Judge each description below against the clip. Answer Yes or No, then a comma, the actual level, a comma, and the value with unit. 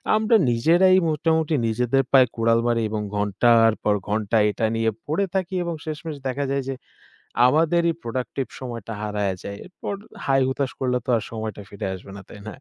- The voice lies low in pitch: Yes, low, 125 Hz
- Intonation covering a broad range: Yes, wide, 5.8 semitones